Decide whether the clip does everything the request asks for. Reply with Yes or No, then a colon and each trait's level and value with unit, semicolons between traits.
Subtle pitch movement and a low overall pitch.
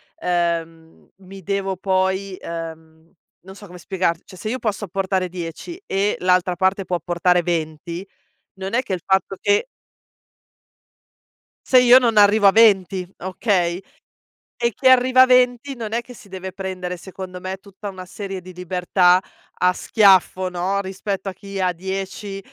No: narrow, 2.0 semitones; high, 190 Hz